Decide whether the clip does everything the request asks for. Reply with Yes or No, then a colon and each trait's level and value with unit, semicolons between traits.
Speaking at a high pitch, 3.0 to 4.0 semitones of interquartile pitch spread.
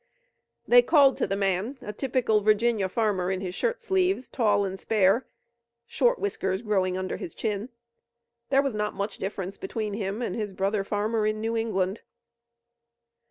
Yes: high, 210 Hz; average, 3.6 semitones